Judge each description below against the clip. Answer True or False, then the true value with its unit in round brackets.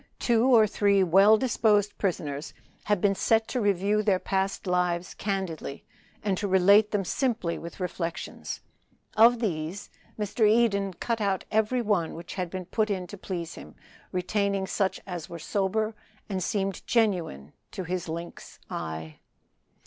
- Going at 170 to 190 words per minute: False (150 wpm)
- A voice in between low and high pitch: False (195 Hz)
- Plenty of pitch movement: False (3.2 semitones)